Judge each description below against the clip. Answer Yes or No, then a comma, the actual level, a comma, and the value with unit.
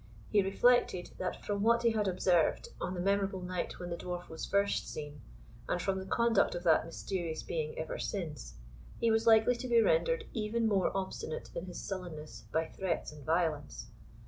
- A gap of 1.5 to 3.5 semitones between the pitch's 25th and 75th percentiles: No, average, 4.3 semitones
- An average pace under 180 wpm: No, average, 185 wpm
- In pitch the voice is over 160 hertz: Yes, medium, 185 Hz